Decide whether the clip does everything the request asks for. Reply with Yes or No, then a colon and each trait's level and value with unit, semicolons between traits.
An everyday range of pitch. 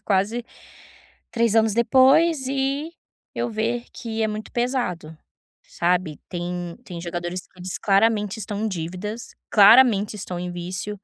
Yes: average, 4.7 semitones